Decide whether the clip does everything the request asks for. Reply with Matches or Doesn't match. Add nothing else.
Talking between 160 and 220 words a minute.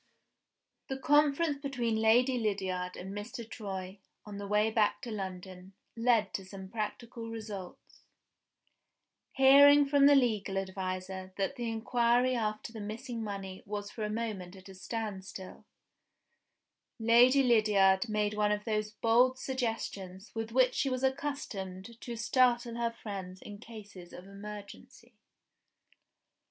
Doesn't match